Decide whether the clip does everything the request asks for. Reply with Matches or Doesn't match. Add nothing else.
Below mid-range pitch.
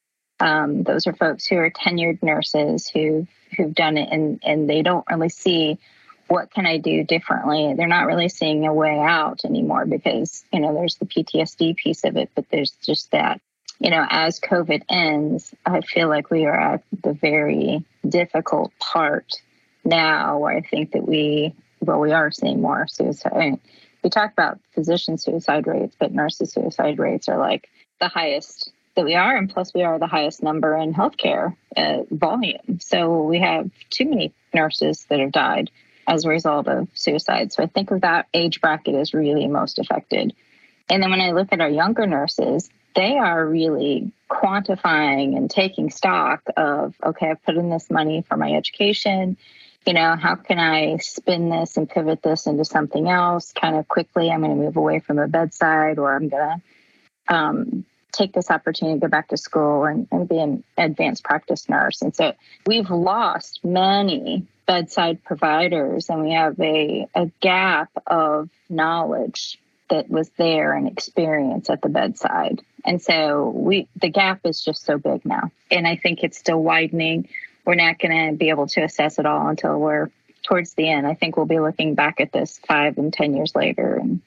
Doesn't match